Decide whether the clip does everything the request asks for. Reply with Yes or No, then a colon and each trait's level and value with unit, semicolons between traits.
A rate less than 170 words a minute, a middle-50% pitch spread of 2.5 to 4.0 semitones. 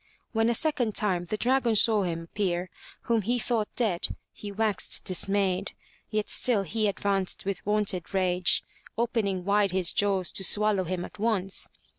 Yes: average, 160 wpm; average, 2.9 semitones